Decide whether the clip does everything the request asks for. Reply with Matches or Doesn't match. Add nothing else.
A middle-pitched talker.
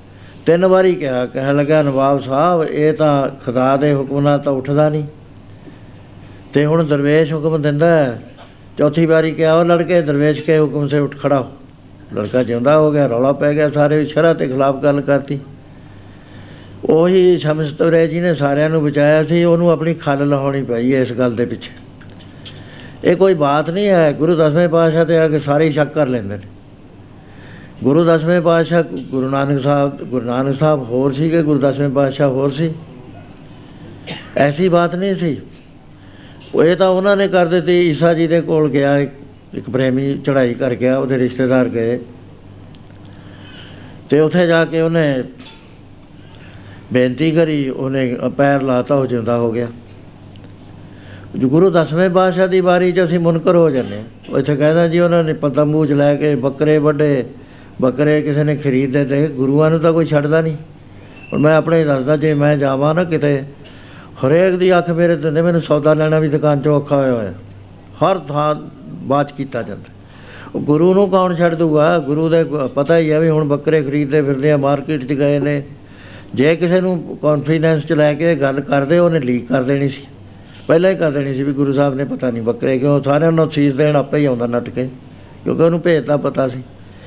Matches